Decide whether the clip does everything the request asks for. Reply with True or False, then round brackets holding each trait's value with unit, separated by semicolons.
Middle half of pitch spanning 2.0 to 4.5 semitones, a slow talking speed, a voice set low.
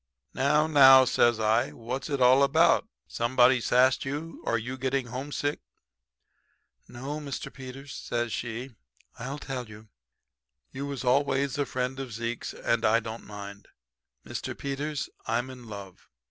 False (2.9 semitones; 145 wpm; 130 Hz)